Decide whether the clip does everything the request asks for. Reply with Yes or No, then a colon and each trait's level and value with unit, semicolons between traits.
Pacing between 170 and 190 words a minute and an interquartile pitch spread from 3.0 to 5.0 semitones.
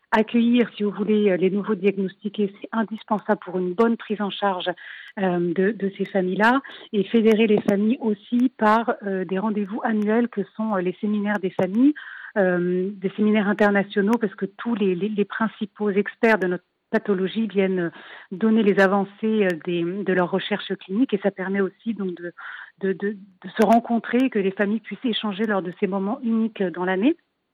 No: average, 180 wpm; narrow, 2.5 semitones